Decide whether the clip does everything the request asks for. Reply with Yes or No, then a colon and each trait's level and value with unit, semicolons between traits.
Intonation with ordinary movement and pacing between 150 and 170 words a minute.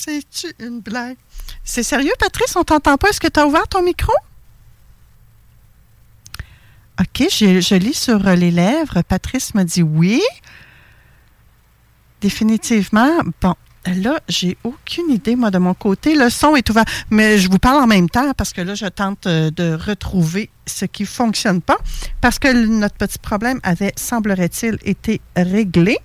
No: wide, 5.7 semitones; average, 160 wpm